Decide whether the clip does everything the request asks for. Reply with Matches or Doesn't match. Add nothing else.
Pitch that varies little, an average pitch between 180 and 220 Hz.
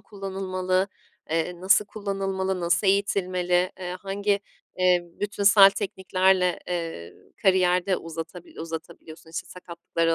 Matches